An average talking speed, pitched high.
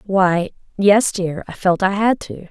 Yes: average, 145 wpm; high, 195 Hz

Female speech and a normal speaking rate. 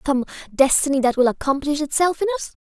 Yes: female; average, 180 wpm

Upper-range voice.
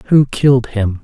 No: low, 120 Hz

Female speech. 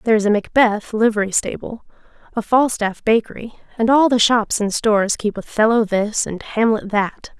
Yes: female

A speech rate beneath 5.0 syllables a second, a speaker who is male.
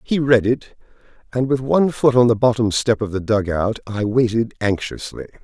No: 5.1 syllables/s; male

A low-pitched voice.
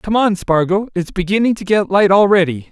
No: high, 195 Hz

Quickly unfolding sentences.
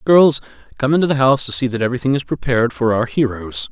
Yes: fast, 225 wpm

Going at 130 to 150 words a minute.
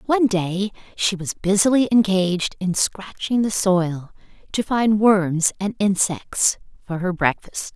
Yes: average, 140 wpm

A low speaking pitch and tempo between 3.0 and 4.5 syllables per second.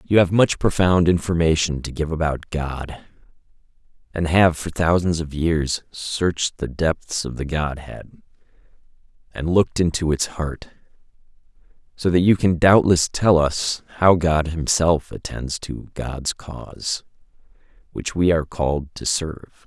Yes: very low, 80 Hz; 4.2 syllables/s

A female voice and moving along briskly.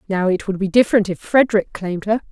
Yes: female; fast, 235 wpm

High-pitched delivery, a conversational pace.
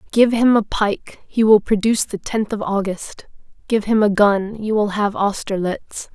Yes: high, 210 Hz; average, 185 wpm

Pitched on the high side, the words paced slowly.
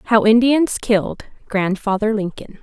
Yes: high, 215 Hz; slow, 115 wpm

